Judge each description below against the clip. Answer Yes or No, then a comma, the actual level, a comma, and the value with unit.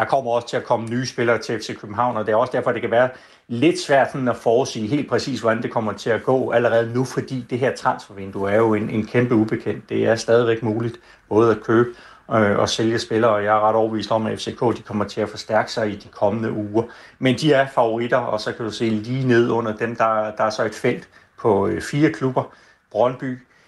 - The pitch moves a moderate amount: No, narrow, 2.3 semitones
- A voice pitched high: No, low, 115 Hz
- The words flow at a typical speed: No, fast, 245 wpm